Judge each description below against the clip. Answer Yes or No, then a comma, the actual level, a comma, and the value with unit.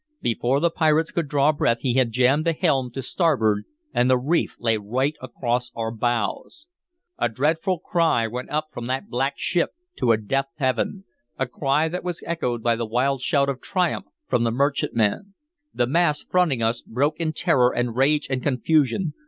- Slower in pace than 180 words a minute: No, average, 185 wpm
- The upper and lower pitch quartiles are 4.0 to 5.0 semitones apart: Yes, average, 4.5 semitones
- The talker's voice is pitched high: No, low, 135 Hz